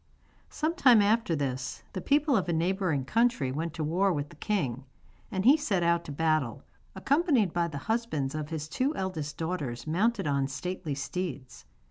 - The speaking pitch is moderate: Yes, medium, 170 Hz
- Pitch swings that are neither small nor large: No, wide, 6.4 semitones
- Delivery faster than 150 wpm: Yes, average, 175 wpm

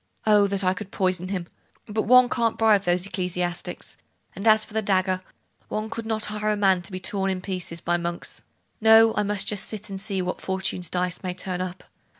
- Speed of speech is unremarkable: No, fast, 215 wpm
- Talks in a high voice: Yes, high, 195 Hz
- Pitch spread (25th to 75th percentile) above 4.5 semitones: No, average, 2.7 semitones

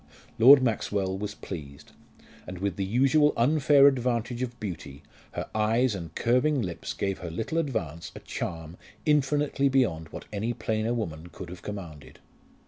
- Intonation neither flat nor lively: No, wide, 6.8 semitones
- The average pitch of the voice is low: Yes, low, 110 Hz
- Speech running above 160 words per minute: No, average, 150 wpm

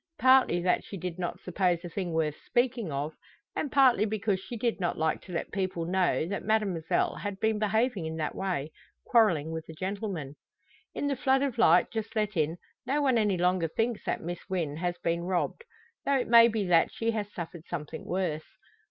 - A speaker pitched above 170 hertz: Yes, high, 190 Hz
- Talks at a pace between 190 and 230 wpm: Yes, average, 200 wpm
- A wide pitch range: No, average, 4.9 semitones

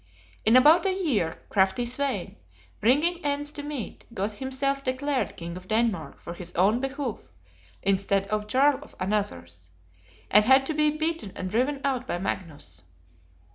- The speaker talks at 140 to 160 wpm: Yes, average, 155 wpm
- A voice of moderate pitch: No, high, 245 Hz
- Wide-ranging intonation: Yes, wide, 6.6 semitones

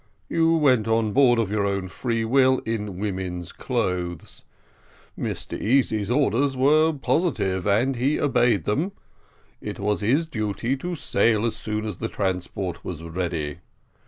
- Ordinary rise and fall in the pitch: No, wide, 5.7 semitones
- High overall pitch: No, low, 110 Hz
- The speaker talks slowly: No, average, 145 wpm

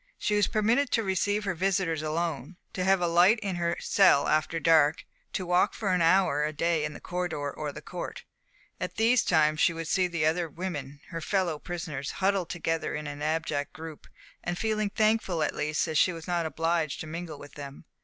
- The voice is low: No, medium, 170 Hz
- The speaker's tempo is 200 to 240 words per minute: Yes, fast, 205 wpm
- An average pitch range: Yes, average, 3.4 semitones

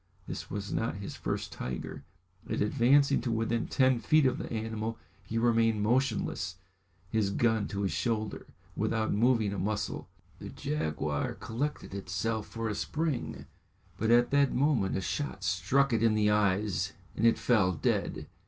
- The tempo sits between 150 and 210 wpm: Yes, average, 160 wpm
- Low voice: Yes, low, 110 Hz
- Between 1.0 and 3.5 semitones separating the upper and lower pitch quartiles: Yes, average, 3.1 semitones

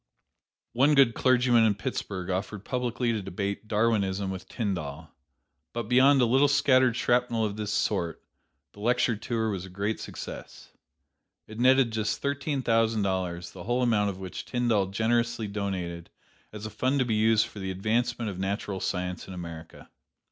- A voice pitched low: Yes, low, 110 Hz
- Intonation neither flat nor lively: Yes, average, 4.1 semitones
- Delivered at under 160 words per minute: No, average, 165 wpm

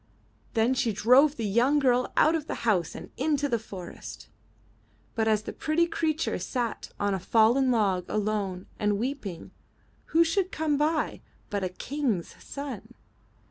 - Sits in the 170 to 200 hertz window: No, high, 240 Hz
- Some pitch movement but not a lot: No, wide, 5.8 semitones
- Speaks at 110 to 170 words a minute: Yes, average, 160 wpm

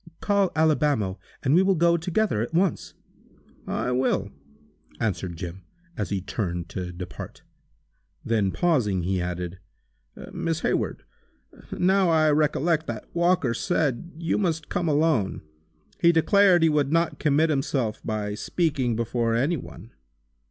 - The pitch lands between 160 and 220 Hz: No, medium, 145 Hz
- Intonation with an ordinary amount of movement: No, wide, 8.1 semitones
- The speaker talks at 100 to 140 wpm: Yes, slow, 135 wpm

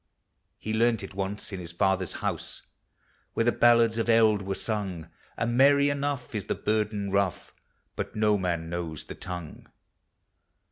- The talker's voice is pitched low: Yes, low, 105 Hz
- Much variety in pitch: No, average, 3.5 semitones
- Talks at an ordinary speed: Yes, average, 170 wpm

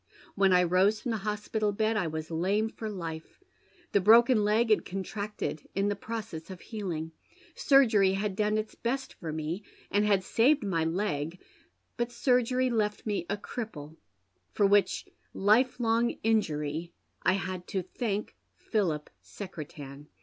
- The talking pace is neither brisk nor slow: Yes, average, 150 wpm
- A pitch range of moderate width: Yes, average, 4.1 semitones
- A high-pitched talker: Yes, high, 205 Hz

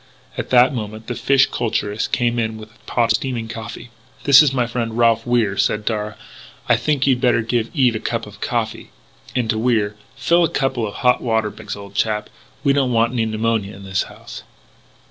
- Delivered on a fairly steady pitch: Yes, narrow, 2.3 semitones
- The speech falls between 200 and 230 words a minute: Yes, fast, 205 wpm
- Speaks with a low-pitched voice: Yes, low, 115 Hz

